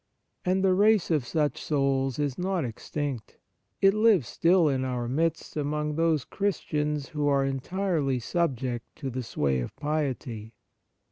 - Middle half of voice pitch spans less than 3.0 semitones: No, average, 4.3 semitones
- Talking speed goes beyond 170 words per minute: No, average, 145 wpm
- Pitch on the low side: No, medium, 150 Hz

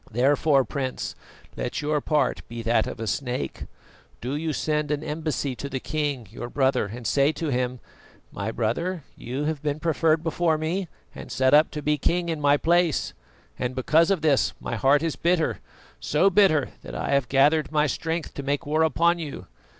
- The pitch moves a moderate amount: Yes, average, 3.4 semitones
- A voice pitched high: No, medium, 150 Hz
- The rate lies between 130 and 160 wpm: No, average, 190 wpm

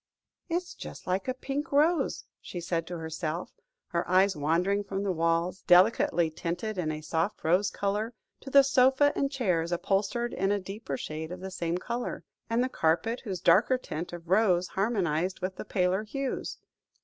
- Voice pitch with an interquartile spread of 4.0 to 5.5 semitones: Yes, average, 5.0 semitones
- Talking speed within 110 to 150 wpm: No, average, 175 wpm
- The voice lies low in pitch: No, high, 190 Hz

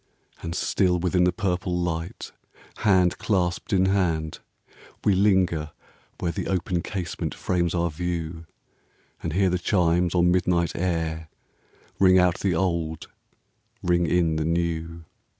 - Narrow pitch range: Yes, narrow, 1.8 semitones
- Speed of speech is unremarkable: No, slow, 130 wpm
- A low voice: Yes, very low, 90 Hz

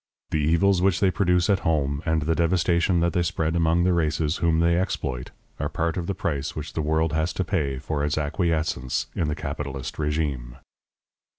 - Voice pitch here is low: Yes, very low, 80 Hz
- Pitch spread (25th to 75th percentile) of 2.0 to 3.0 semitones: Yes, narrow, 2.6 semitones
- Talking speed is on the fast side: No, average, 195 wpm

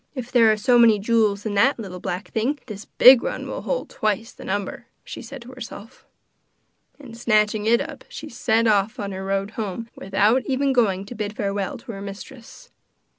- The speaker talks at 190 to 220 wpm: Yes, average, 200 wpm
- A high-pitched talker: Yes, high, 220 Hz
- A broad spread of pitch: No, average, 3.2 semitones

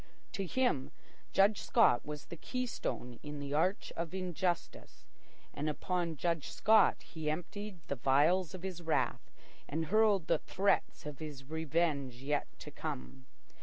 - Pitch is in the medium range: Yes, medium, 165 Hz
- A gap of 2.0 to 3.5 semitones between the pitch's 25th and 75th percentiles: No, average, 4.3 semitones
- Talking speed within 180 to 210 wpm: No, average, 145 wpm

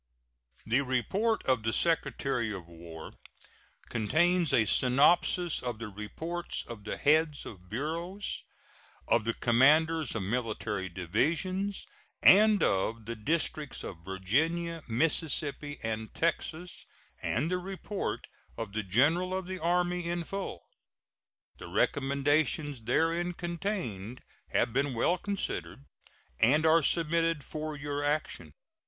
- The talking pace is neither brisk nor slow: No, slow, 120 wpm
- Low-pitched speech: No, medium, 145 Hz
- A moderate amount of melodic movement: No, wide, 7.1 semitones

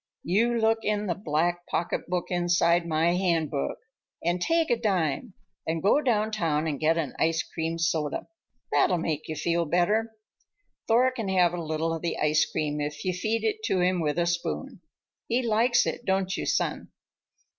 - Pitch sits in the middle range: Yes, medium, 175 Hz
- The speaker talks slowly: No, average, 175 wpm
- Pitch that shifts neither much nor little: Yes, average, 4.7 semitones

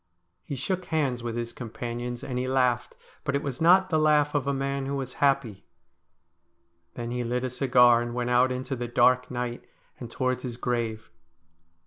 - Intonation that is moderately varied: No, narrow, 2.3 semitones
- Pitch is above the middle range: No, low, 125 Hz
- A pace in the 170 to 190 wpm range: Yes, average, 185 wpm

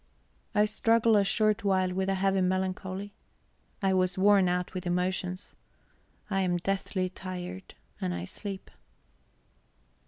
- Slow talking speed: Yes, slow, 130 wpm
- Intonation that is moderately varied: No, narrow, 1.5 semitones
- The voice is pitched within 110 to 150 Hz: No, high, 190 Hz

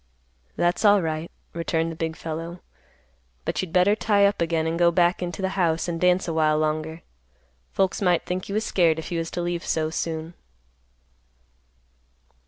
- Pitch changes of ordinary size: No, narrow, 2.0 semitones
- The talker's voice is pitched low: No, medium, 170 Hz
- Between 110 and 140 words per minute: No, average, 175 wpm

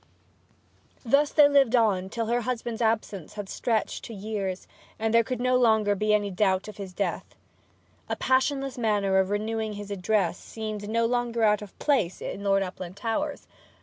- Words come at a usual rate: Yes, average, 170 wpm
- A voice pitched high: Yes, high, 215 Hz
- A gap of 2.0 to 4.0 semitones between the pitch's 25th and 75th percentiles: Yes, average, 2.9 semitones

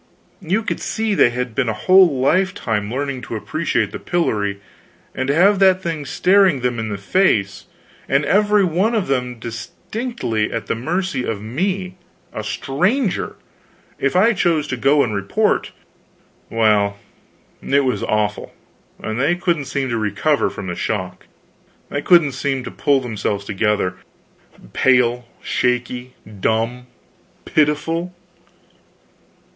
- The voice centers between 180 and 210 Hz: No, low, 135 Hz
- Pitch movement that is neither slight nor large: No, wide, 7.8 semitones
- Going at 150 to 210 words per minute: No, slow, 135 wpm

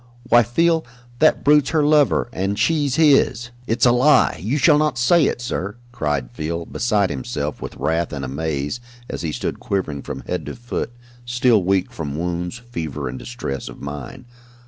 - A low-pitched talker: Yes, low, 110 Hz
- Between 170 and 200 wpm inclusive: Yes, average, 180 wpm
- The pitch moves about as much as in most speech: No, wide, 8.2 semitones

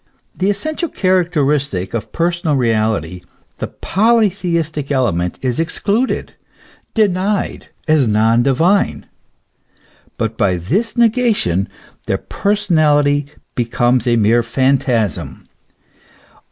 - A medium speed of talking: No, slow, 95 wpm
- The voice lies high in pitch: No, medium, 145 Hz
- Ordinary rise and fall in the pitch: No, wide, 8.5 semitones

